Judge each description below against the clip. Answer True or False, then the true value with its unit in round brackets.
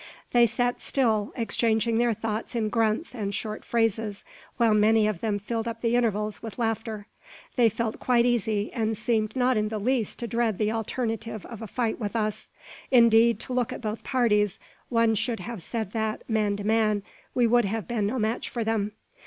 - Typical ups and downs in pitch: False (1.8 semitones)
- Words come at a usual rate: True (195 wpm)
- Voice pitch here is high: True (225 Hz)